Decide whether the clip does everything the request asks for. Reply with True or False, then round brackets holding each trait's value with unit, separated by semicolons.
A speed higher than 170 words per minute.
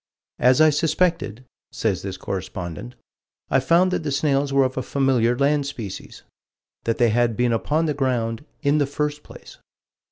False (165 wpm)